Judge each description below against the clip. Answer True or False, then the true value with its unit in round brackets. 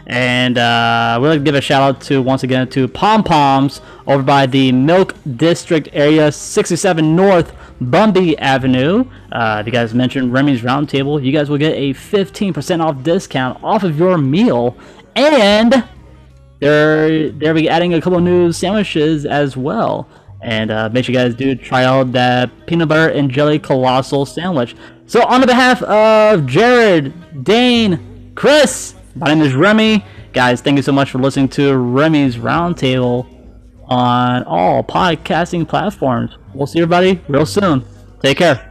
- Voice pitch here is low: False (145 Hz)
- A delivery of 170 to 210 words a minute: False (160 wpm)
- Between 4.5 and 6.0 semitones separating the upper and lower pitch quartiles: True (5.2 semitones)